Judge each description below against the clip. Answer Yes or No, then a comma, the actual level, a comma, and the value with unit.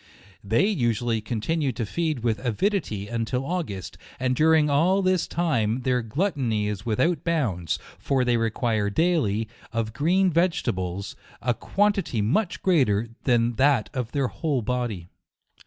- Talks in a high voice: No, low, 125 Hz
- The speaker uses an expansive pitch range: Yes, wide, 6.7 semitones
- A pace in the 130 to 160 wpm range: Yes, average, 145 wpm